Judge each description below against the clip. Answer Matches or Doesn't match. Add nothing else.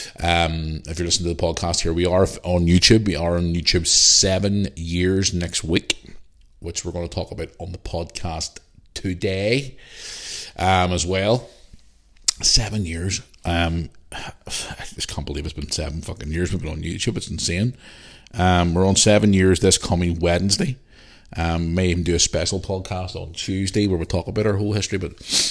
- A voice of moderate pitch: Doesn't match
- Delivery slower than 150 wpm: Doesn't match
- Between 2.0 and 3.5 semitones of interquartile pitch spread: Matches